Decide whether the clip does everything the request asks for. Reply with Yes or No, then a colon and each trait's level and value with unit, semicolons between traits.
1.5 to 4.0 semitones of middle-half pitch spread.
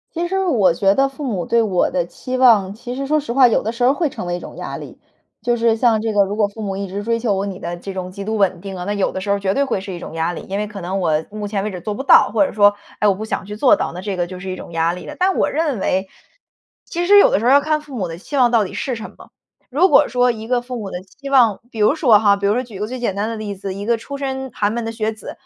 No: average, 4.5 semitones